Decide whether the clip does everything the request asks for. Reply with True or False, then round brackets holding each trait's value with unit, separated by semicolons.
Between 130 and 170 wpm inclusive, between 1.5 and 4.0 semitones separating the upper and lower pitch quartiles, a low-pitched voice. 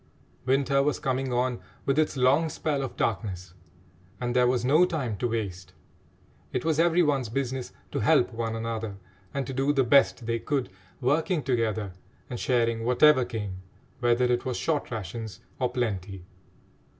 True (160 wpm; 3.4 semitones; 125 Hz)